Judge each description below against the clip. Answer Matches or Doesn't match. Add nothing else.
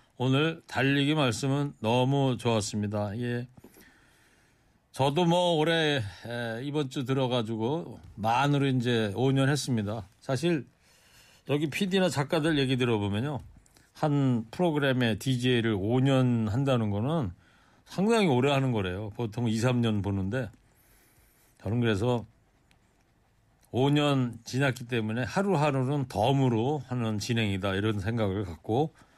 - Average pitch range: Matches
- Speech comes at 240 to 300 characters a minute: Matches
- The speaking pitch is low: Matches